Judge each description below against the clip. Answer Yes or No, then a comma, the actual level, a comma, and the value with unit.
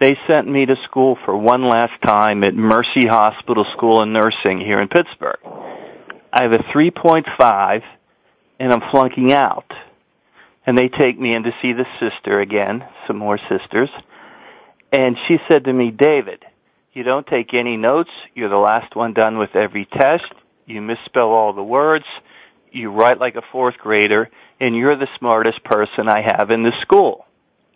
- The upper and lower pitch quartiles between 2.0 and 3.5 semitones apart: Yes, average, 3.1 semitones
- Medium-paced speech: Yes, average, 170 wpm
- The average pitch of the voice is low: Yes, low, 120 Hz